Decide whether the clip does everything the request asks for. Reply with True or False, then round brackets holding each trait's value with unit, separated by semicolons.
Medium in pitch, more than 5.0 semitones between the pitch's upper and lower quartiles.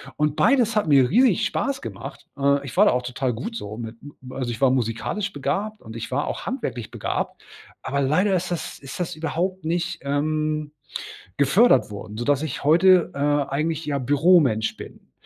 True (145 Hz; 5.4 semitones)